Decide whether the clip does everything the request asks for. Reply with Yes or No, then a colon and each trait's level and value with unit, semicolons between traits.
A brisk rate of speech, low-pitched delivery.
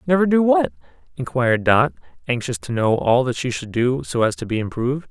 Yes: fast, 210 wpm; low, 125 Hz